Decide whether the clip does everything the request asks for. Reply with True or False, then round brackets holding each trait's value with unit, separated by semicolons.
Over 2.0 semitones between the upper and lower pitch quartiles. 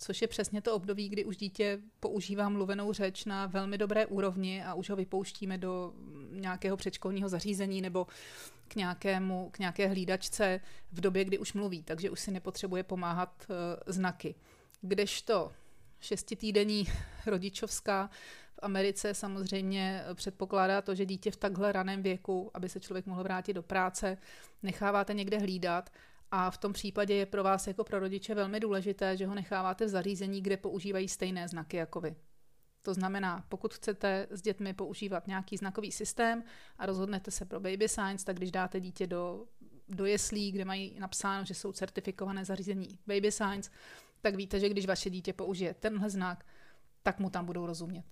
False (1.4 semitones)